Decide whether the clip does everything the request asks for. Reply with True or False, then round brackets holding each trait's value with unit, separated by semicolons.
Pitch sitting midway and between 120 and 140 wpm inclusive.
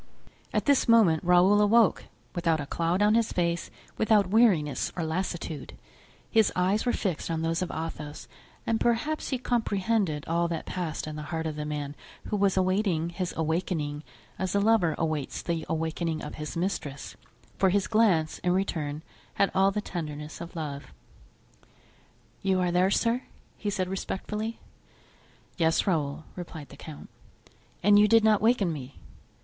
False (180 Hz; 160 wpm)